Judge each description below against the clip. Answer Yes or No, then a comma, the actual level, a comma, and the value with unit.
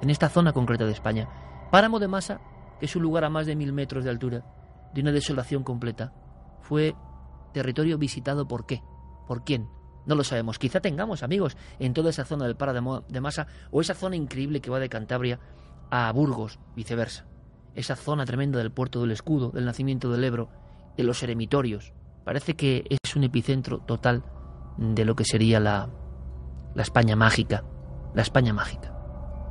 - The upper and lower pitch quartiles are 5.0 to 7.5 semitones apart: Yes, average, 5.3 semitones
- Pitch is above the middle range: No, low, 125 Hz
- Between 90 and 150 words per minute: No, average, 175 wpm